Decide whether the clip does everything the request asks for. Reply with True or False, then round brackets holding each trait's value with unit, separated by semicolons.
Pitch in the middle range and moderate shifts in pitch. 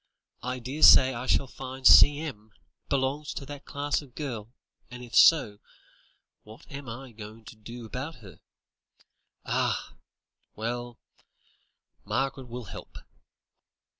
False (125 Hz; 3.1 semitones)